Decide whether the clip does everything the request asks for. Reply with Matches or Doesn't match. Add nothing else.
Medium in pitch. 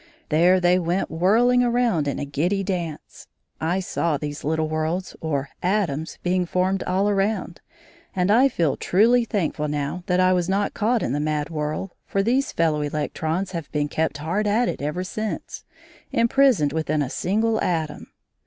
Matches